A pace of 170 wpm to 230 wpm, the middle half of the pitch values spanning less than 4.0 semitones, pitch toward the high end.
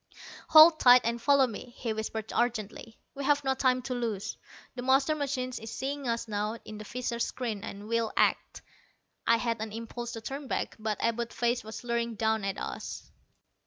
Yes: average, 185 wpm; narrow, 2.6 semitones; high, 235 Hz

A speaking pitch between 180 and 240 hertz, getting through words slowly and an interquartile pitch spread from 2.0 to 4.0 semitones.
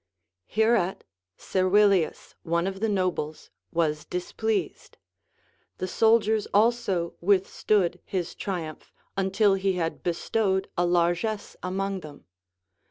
Yes: high, 190 Hz; slow, 100 wpm; average, 3.0 semitones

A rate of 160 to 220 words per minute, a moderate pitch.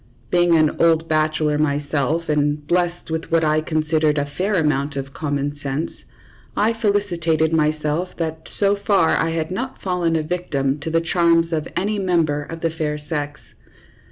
Yes: average, 165 wpm; medium, 160 Hz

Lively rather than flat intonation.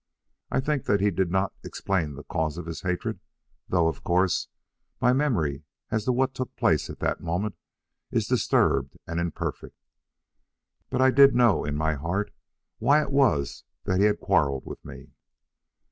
Yes: wide, 7.5 semitones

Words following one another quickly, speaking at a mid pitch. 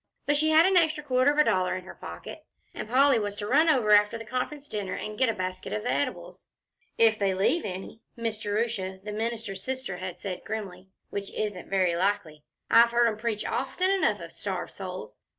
No: fast, 210 wpm; high, 215 Hz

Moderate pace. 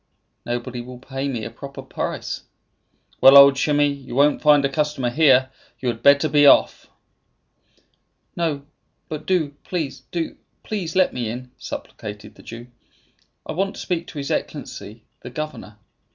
Yes: average, 155 wpm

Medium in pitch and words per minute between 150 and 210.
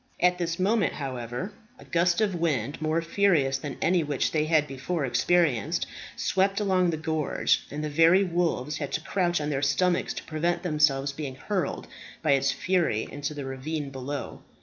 Yes: medium, 155 Hz; average, 175 wpm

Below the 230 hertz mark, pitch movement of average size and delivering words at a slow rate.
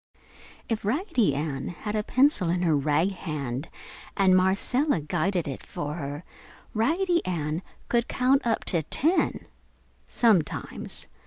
No: medium, 185 Hz; wide, 7.8 semitones; slow, 130 wpm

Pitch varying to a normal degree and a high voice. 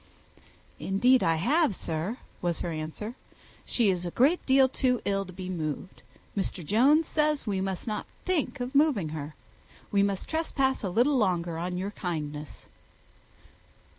No: wide, 7.1 semitones; high, 200 Hz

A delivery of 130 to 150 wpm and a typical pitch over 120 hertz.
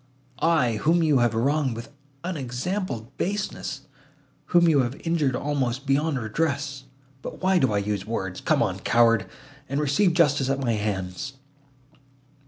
Yes: slow, 135 wpm; low, 135 Hz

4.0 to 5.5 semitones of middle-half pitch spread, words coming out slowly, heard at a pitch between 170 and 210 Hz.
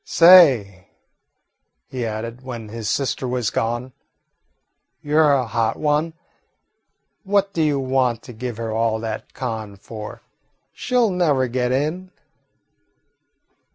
No: average, 4.7 semitones; slow, 125 wpm; low, 125 Hz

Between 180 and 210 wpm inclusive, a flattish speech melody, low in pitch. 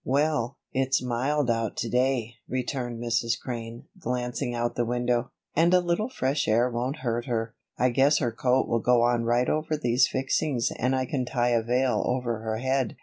Yes: average, 190 wpm; narrow, 2.1 semitones; low, 125 Hz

